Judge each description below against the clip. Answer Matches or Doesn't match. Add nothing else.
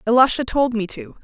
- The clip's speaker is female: Matches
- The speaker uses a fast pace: Doesn't match